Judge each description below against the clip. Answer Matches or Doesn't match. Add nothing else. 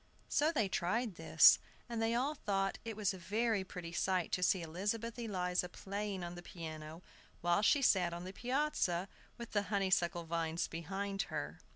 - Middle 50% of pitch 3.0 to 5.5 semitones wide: Matches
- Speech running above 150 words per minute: Matches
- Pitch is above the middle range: Matches